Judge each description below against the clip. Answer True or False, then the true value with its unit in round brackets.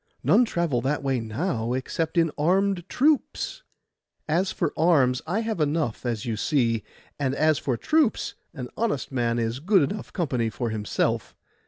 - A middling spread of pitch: False (6.7 semitones)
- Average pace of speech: True (160 wpm)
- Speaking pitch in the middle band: True (145 Hz)